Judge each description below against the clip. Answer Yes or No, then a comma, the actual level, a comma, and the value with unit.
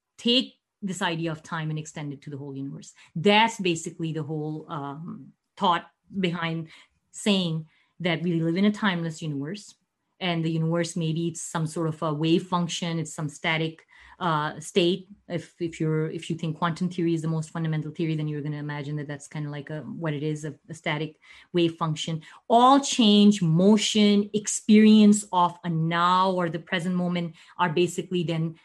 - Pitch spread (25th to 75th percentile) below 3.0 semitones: Yes, narrow, 2.6 semitones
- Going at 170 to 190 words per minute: Yes, average, 185 wpm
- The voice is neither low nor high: Yes, medium, 170 Hz